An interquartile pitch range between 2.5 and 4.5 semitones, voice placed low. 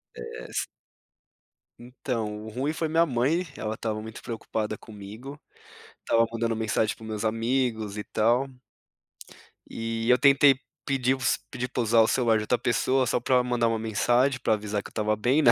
Yes: average, 2.8 semitones; low, 115 Hz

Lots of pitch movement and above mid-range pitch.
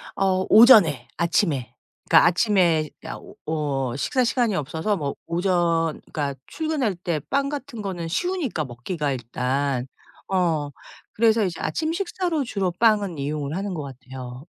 No: wide, 7.1 semitones; medium, 170 Hz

